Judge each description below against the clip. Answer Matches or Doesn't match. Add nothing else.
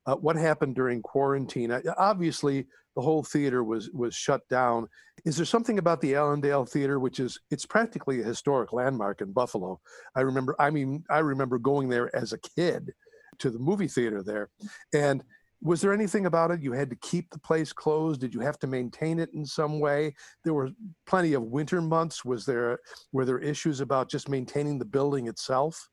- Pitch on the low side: Doesn't match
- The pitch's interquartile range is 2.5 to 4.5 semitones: Matches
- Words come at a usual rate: Matches